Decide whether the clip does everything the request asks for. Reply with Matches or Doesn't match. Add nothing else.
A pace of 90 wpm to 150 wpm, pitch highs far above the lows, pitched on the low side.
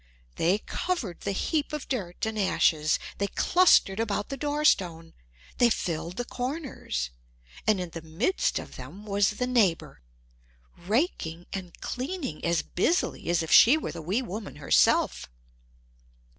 Doesn't match